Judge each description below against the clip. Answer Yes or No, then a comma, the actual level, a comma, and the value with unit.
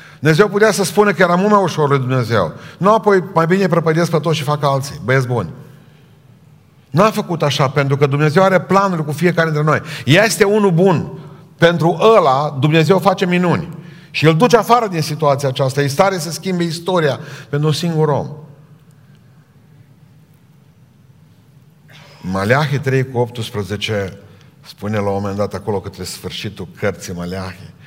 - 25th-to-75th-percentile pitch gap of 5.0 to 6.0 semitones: No, average, 3.9 semitones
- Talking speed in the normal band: Yes, average, 160 wpm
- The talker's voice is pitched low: No, medium, 150 Hz